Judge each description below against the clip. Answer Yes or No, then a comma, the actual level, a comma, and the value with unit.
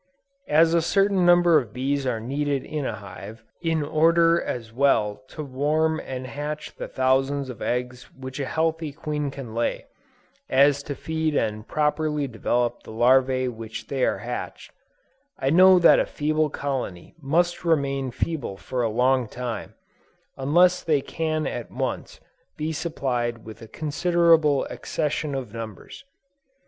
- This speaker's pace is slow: No, average, 150 wpm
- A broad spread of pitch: No, average, 4.1 semitones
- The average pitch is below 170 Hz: Yes, medium, 140 Hz